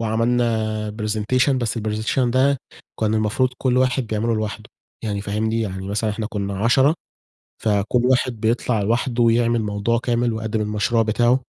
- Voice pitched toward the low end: Yes, low, 110 Hz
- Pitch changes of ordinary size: No, narrow, 2.2 semitones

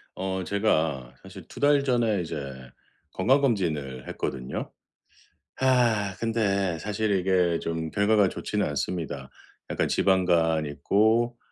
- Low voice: Yes, very low, 95 Hz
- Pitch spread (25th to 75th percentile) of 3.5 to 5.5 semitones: Yes, average, 5.2 semitones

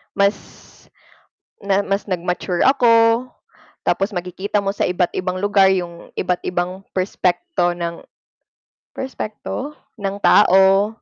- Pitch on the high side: Yes, high, 195 Hz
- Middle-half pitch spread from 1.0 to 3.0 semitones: Yes, narrow, 2.5 semitones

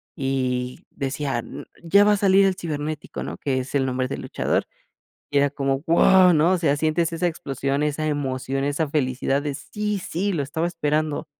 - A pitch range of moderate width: Yes, average, 3.7 semitones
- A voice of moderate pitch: Yes, medium, 150 Hz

